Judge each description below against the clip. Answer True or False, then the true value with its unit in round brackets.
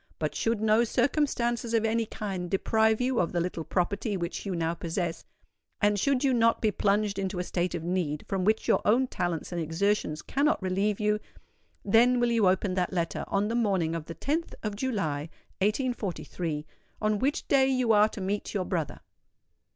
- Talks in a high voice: True (205 Hz)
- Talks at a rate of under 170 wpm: False (180 wpm)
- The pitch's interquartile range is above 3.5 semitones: True (4.4 semitones)